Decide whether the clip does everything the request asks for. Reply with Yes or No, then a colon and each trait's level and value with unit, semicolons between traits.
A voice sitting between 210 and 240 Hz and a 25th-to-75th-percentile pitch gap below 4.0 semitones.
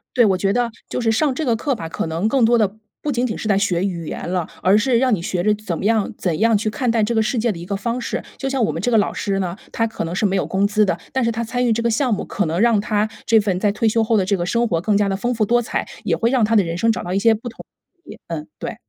Yes: high, 215 Hz; average, 3.3 semitones